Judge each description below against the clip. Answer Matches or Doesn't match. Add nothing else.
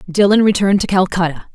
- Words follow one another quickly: Doesn't match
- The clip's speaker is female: Matches